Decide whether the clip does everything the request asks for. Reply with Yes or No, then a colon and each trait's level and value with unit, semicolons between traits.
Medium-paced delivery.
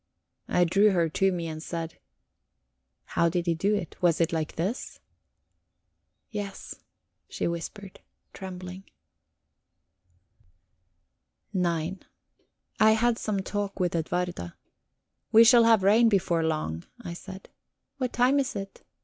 No: slow, 125 wpm